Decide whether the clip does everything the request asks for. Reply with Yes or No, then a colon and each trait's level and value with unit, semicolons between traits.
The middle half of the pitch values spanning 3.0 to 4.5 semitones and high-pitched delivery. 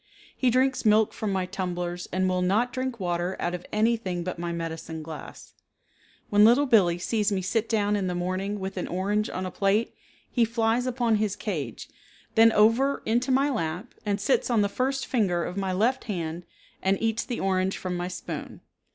Yes: average, 4.1 semitones; high, 200 Hz